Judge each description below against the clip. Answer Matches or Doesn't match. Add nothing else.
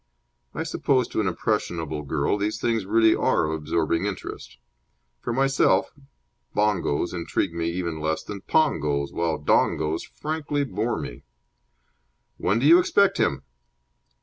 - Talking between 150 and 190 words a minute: Doesn't match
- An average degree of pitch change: Doesn't match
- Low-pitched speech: Matches